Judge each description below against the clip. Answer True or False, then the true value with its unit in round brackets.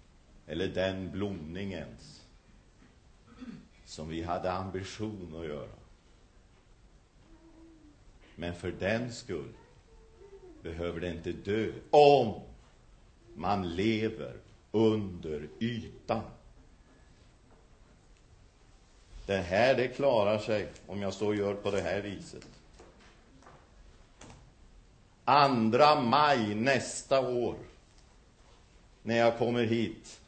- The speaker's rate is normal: False (85 wpm)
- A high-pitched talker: False (100 Hz)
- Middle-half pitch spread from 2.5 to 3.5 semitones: False (5.0 semitones)